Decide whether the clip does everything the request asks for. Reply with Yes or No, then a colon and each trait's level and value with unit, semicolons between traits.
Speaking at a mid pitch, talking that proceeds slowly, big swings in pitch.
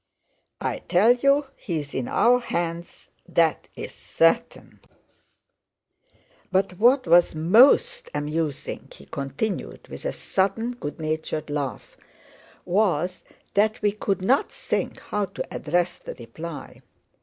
Yes: medium, 180 Hz; slow, 120 wpm; wide, 5.9 semitones